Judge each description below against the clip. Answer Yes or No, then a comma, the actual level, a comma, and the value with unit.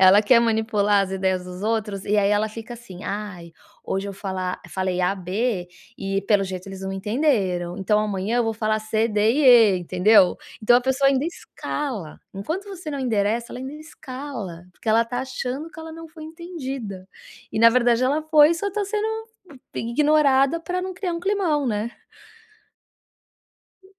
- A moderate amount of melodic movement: No, wide, 6.5 semitones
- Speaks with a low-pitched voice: No, high, 225 Hz